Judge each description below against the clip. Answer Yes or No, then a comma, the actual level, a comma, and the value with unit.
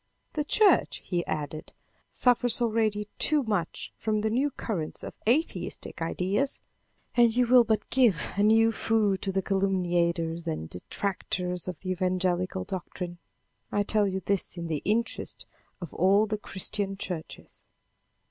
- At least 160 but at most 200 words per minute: No, average, 145 wpm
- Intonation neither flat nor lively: Yes, average, 3.9 semitones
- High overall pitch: Yes, high, 195 Hz